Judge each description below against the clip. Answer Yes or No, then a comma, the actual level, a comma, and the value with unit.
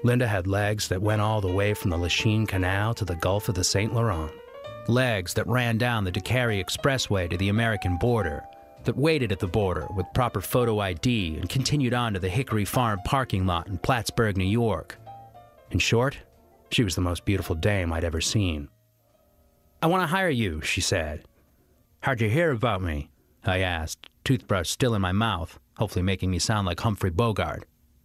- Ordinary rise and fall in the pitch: Yes, average, 4.5 semitones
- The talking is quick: No, average, 190 wpm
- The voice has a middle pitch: No, low, 105 Hz